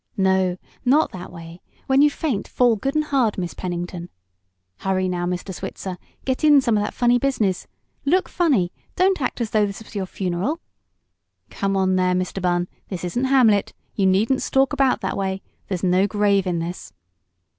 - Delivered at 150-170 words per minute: No, average, 180 wpm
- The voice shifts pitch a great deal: Yes, wide, 6.1 semitones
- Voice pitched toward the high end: Yes, high, 195 Hz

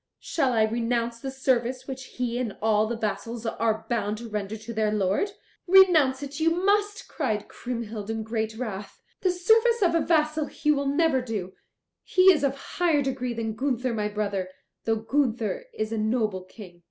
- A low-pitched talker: No, high, 235 Hz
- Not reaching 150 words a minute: No, average, 180 wpm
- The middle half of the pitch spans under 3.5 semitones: No, average, 4.9 semitones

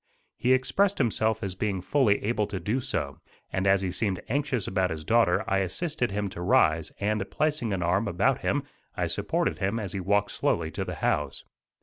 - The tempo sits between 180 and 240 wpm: Yes, average, 200 wpm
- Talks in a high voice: No, low, 100 Hz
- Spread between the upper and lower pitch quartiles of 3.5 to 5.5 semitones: Yes, average, 3.9 semitones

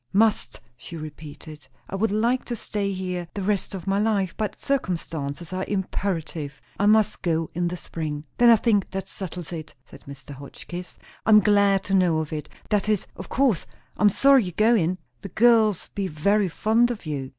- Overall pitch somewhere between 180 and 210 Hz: Yes, high, 190 Hz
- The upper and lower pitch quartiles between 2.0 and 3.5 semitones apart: No, average, 4.5 semitones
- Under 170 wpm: No, average, 185 wpm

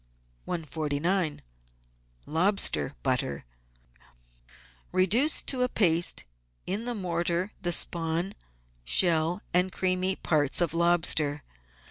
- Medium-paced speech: No, slow, 90 wpm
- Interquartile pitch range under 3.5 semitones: Yes, average, 2.8 semitones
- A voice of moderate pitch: Yes, medium, 175 Hz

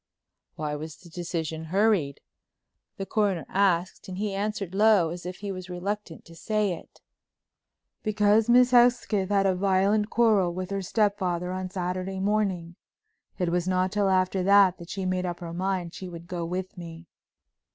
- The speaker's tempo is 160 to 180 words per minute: Yes, average, 170 wpm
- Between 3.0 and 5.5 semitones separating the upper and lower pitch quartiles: No, narrow, 2.5 semitones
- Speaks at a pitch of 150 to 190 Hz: Yes, medium, 185 Hz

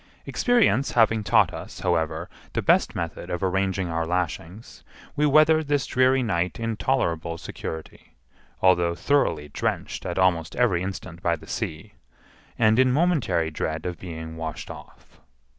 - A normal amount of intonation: No, wide, 6.9 semitones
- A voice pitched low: Yes, very low, 90 Hz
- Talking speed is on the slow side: No, average, 145 wpm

